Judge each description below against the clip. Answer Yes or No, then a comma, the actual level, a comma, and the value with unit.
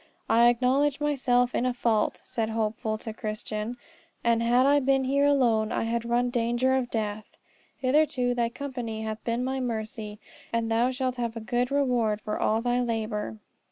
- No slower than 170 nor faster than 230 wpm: Yes, average, 180 wpm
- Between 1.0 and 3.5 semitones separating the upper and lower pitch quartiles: Yes, narrow, 2.5 semitones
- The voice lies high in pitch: Yes, high, 240 Hz